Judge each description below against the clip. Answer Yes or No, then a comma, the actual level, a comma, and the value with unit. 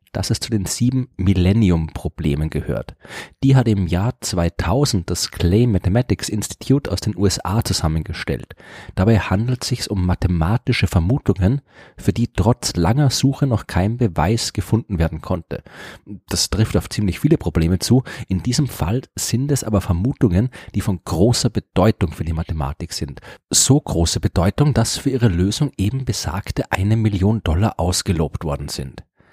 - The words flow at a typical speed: Yes, average, 155 wpm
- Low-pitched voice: Yes, low, 100 Hz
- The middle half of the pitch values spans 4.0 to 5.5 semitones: Yes, average, 4.8 semitones